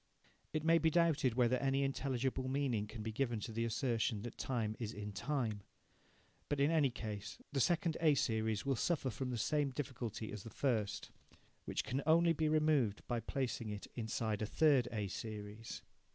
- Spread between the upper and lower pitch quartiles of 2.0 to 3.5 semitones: No, average, 4.4 semitones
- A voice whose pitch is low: Yes, low, 125 Hz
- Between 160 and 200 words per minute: Yes, average, 180 wpm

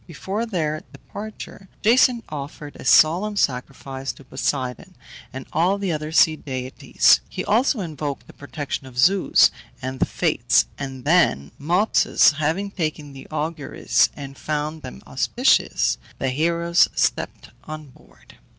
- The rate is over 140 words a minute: No, slow, 135 wpm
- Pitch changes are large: No, average, 4.5 semitones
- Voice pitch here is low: No, medium, 155 Hz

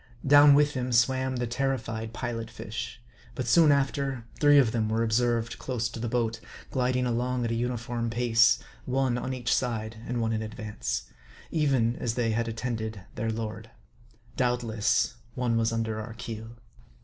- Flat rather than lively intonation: Yes, narrow, 2.1 semitones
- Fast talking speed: No, average, 165 wpm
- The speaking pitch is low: Yes, low, 120 Hz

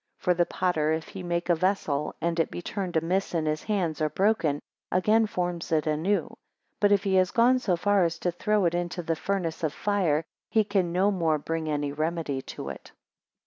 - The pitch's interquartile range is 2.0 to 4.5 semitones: Yes, average, 3.6 semitones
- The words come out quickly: Yes, fast, 210 wpm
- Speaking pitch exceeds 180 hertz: No, medium, 175 Hz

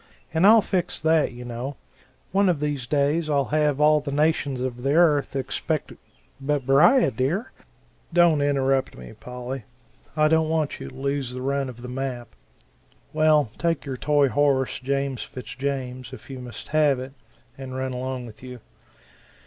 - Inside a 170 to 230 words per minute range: Yes, average, 175 wpm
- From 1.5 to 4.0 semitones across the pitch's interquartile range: Yes, average, 2.9 semitones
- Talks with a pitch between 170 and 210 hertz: No, medium, 140 Hz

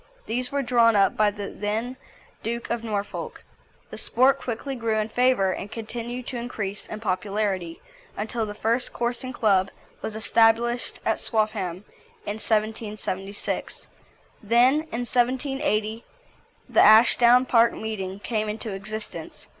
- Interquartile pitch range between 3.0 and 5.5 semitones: No, narrow, 2.5 semitones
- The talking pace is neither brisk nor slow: No, slow, 130 wpm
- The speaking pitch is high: Yes, high, 220 Hz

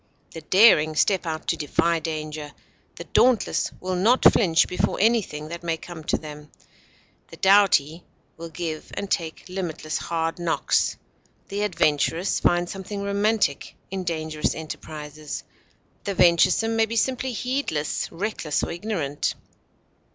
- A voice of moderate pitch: Yes, medium, 170 Hz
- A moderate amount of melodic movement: Yes, average, 4.3 semitones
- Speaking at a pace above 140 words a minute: No, slow, 135 wpm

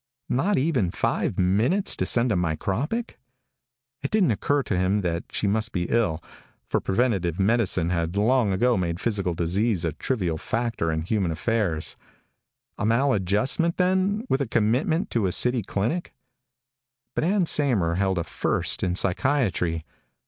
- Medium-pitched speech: No, low, 105 Hz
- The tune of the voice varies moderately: No, wide, 6.3 semitones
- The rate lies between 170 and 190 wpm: No, average, 150 wpm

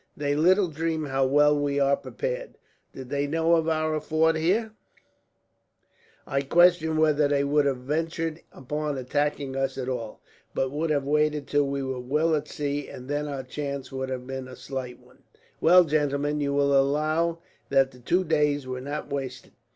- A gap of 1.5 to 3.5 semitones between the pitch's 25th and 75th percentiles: Yes, narrow, 2.6 semitones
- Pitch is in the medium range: Yes, medium, 145 Hz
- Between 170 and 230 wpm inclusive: Yes, average, 180 wpm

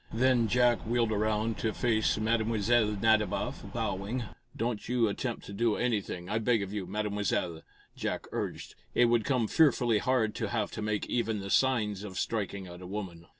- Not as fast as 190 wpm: Yes, average, 175 wpm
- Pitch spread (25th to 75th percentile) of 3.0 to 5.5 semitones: No, narrow, 2.5 semitones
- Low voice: Yes, low, 110 Hz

